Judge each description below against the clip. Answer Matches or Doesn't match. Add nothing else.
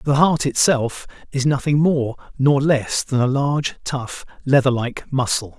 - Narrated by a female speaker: Doesn't match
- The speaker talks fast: Doesn't match